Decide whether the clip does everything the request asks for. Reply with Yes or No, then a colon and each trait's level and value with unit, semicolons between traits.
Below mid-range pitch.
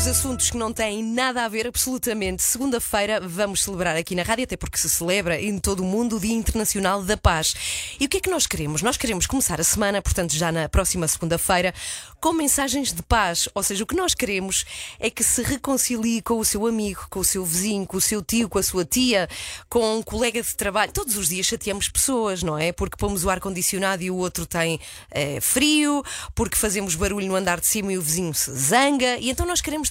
No: high, 205 Hz